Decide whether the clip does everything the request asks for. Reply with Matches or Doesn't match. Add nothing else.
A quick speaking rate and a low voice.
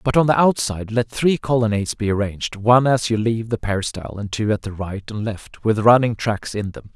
Matches